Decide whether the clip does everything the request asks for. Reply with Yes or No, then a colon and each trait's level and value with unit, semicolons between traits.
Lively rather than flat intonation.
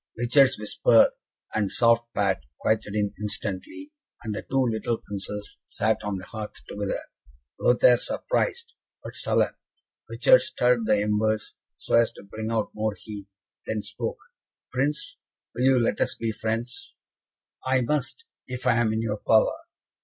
No: average, 2.9 semitones